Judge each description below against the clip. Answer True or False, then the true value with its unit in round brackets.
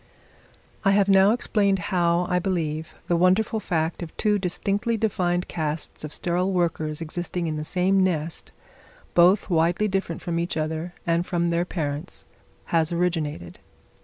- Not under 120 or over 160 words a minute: True (150 wpm)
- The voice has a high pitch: False (175 Hz)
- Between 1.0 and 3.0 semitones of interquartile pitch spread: True (2.7 semitones)